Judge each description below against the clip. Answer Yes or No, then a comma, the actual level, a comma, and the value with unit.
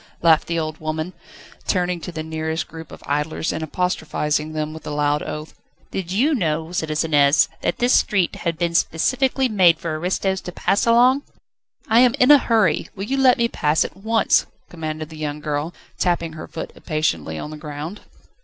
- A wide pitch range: No, average, 3.8 semitones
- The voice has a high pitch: No, medium, 165 Hz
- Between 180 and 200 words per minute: Yes, average, 185 wpm